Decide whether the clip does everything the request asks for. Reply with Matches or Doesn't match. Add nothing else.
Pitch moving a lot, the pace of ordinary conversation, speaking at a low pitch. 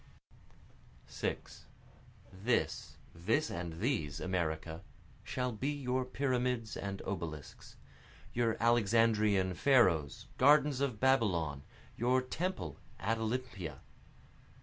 Doesn't match